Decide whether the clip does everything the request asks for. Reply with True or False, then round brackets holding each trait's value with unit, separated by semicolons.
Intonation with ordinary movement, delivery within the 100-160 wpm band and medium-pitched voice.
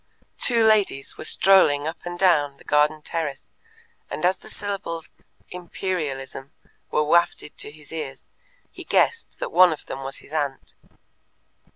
True (4.2 semitones; 150 wpm; 155 Hz)